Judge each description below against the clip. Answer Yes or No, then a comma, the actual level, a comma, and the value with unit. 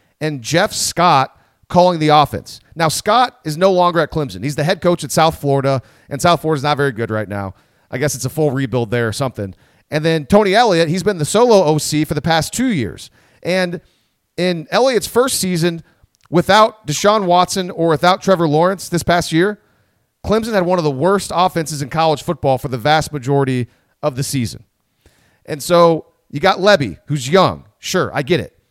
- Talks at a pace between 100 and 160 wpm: No, average, 195 wpm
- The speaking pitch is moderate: Yes, medium, 155 Hz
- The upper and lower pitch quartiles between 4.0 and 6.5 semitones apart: Yes, average, 4.5 semitones